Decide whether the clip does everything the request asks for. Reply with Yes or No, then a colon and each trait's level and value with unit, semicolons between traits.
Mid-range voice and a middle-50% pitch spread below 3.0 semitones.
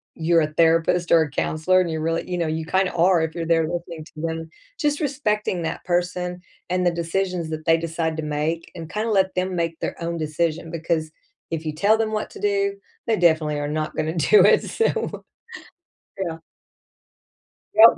Yes: medium, 170 Hz; narrow, 2.4 semitones